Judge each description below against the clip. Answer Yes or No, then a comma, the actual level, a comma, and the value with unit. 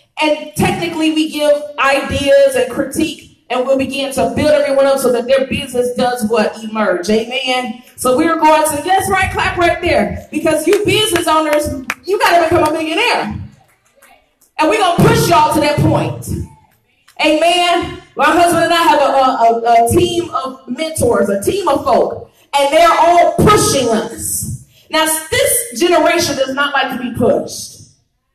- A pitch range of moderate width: Yes, average, 4.1 semitones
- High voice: Yes, very high, 300 Hz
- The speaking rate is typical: Yes, average, 170 wpm